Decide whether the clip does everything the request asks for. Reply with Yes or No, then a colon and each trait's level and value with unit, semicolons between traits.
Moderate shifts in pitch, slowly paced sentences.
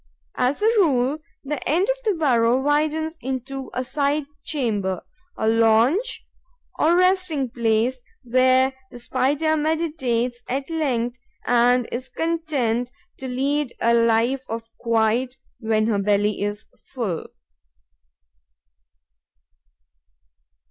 Yes: average, 4.3 semitones; slow, 110 wpm